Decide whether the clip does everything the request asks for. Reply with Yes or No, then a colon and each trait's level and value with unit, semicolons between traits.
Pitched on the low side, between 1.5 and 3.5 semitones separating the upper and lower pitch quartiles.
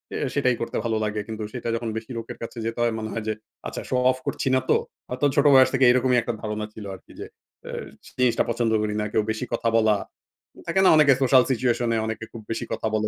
Yes: low, 115 Hz; narrow, 2.5 semitones